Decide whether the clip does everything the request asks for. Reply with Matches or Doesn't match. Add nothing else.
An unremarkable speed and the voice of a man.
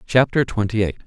Matches